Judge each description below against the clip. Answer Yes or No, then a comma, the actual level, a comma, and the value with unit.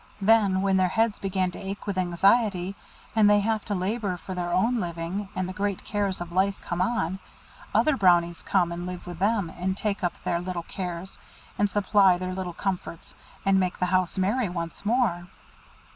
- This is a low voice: No, high, 190 Hz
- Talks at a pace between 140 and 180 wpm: No, average, 190 wpm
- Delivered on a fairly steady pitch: Yes, narrow, 2.3 semitones